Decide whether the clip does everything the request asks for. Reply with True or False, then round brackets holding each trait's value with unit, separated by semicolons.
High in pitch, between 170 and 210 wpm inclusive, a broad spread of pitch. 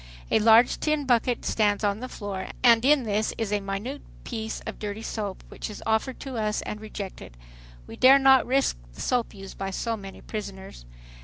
False (220 Hz; 190 wpm; 3.5 semitones)